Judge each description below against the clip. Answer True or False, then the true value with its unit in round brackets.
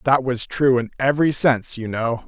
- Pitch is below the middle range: True (125 Hz)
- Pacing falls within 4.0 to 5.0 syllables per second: False (5.4 syllables/s)